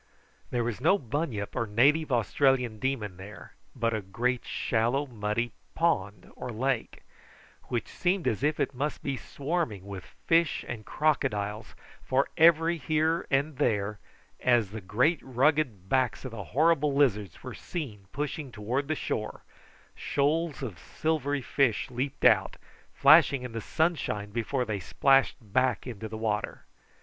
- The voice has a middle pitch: No, low, 125 Hz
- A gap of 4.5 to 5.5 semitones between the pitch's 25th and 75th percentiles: Yes, average, 5.2 semitones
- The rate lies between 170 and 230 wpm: No, average, 145 wpm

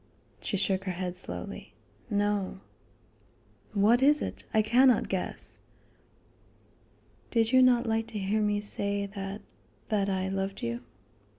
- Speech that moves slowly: Yes, slow, 130 wpm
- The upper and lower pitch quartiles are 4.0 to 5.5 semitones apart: No, narrow, 2.5 semitones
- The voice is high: Yes, high, 205 Hz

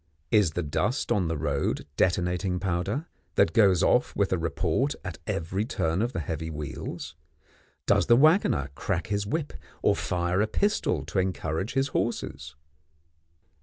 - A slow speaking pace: No, average, 155 wpm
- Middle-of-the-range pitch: No, very low, 90 Hz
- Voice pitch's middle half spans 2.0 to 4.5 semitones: No, average, 5.1 semitones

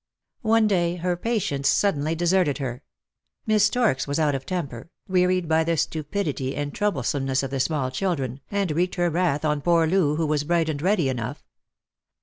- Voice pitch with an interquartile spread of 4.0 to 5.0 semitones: Yes, average, 4.3 semitones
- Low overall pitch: No, medium, 160 Hz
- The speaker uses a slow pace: No, average, 180 wpm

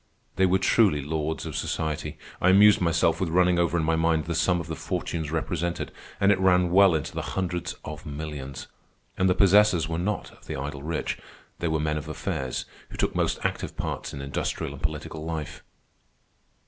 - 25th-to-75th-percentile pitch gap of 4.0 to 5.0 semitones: No, average, 2.8 semitones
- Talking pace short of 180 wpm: No, average, 195 wpm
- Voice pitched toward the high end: No, very low, 80 Hz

